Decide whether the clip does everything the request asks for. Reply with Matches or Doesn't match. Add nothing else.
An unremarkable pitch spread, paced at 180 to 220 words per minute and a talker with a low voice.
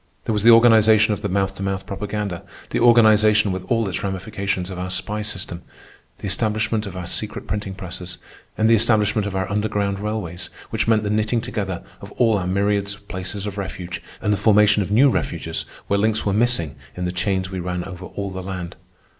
Doesn't match